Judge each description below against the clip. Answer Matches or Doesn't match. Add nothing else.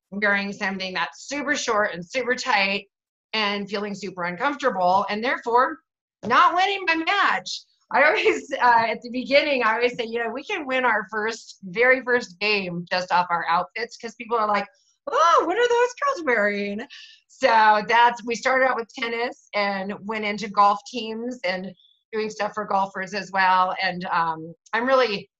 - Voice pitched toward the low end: Doesn't match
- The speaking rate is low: Doesn't match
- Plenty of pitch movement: Doesn't match